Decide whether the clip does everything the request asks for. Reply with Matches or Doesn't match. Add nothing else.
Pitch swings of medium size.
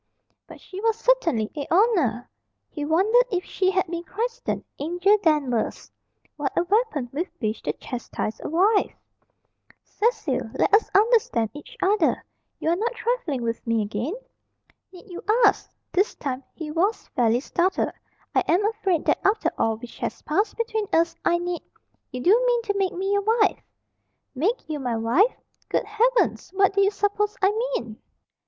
Doesn't match